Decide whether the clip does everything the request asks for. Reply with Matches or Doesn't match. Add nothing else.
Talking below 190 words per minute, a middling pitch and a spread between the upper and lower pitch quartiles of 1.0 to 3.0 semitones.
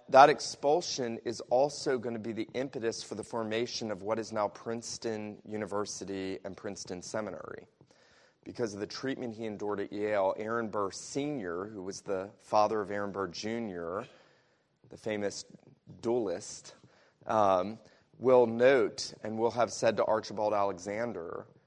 Doesn't match